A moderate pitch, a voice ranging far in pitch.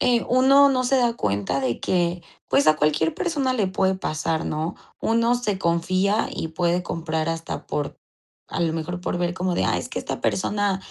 Yes: medium, 180 Hz; wide, 6.0 semitones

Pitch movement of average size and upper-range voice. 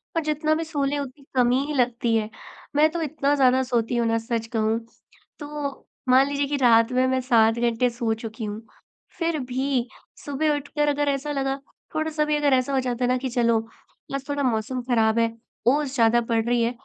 Yes: average, 3.5 semitones; very high, 260 Hz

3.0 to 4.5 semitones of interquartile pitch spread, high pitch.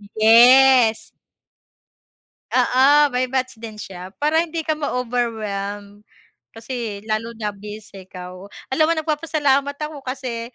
No: average, 4.9 semitones; high, 245 Hz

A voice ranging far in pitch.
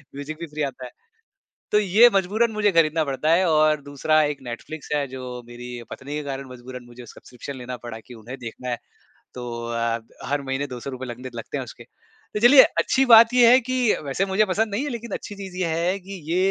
Yes: wide, 7.5 semitones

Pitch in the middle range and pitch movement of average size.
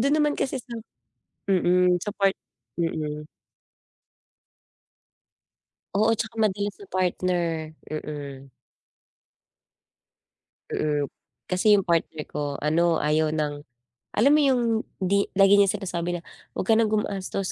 Yes: medium, 180 Hz; average, 4.6 semitones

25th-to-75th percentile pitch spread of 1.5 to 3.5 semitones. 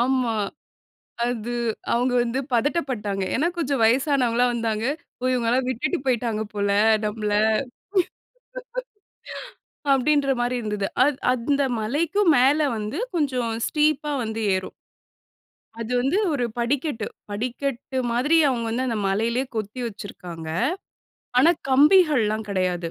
No: average, 3.9 semitones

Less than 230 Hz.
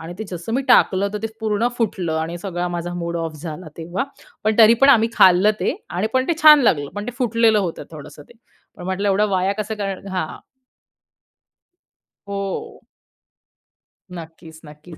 Yes: high, 190 Hz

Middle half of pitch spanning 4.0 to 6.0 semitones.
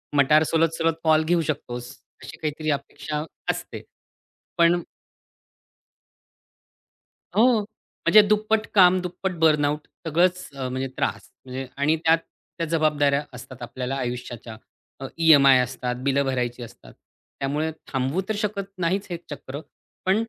Yes: average, 4.4 semitones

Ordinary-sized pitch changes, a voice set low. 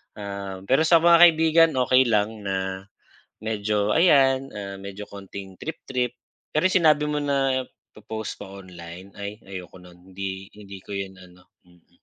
No: wide, 5.7 semitones; low, 105 Hz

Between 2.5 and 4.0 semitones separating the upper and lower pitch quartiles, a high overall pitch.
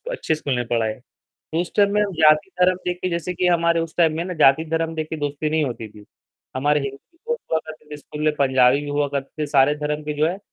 No: average, 2.9 semitones; medium, 155 Hz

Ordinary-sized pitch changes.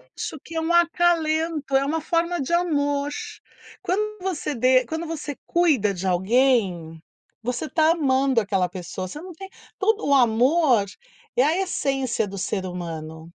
No: wide, 7.9 semitones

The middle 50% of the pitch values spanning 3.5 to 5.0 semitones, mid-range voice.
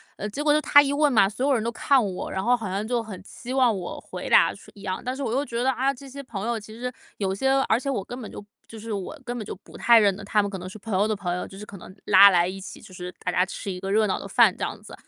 No: average, 4.3 semitones; high, 215 Hz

